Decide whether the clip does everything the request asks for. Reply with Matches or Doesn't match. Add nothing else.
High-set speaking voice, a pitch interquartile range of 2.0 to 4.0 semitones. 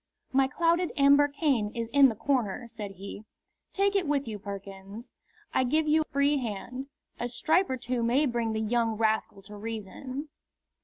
Doesn't match